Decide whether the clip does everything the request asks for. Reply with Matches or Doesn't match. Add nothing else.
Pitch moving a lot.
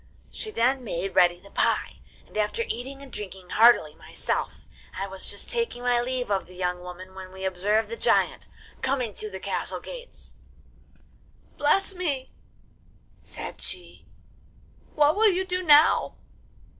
Matches